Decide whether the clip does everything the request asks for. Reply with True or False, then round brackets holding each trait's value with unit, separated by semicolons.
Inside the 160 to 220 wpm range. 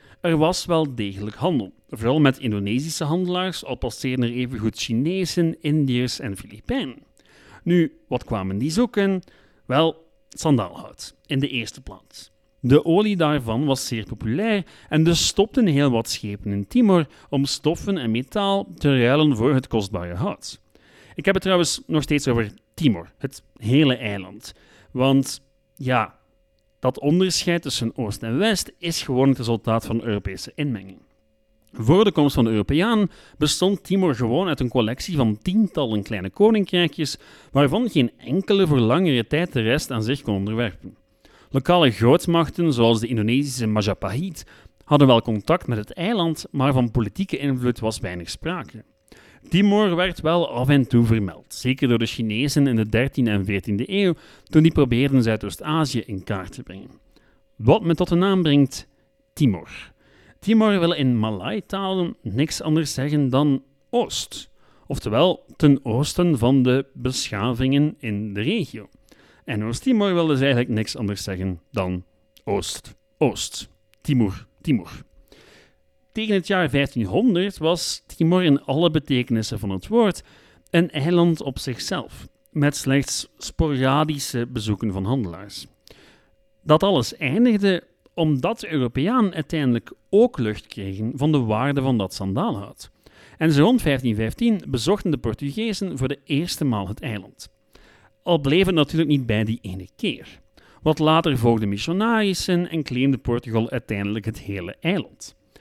False (150 wpm)